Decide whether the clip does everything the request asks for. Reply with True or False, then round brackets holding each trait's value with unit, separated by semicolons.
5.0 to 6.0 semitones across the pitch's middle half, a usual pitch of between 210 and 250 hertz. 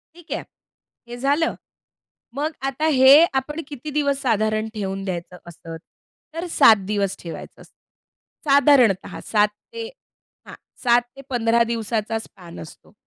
True (5.3 semitones; 235 Hz)